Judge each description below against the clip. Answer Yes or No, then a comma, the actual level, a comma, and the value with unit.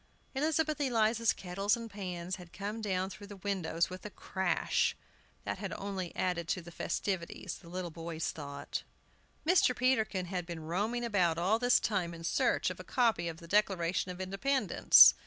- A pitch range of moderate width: Yes, average, 4.1 semitones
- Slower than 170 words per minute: No, average, 175 wpm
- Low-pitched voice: No, high, 190 Hz